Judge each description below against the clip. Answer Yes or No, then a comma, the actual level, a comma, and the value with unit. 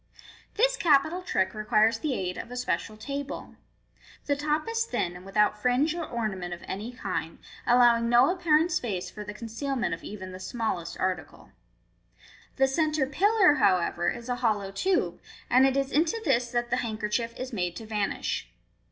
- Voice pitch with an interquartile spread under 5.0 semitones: No, wide, 5.5 semitones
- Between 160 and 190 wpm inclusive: Yes, average, 175 wpm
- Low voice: No, high, 240 Hz